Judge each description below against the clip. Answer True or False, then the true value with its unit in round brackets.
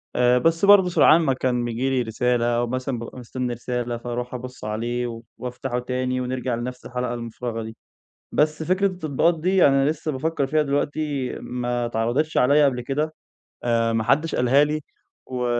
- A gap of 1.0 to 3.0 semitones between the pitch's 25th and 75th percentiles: False (3.5 semitones)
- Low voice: True (125 Hz)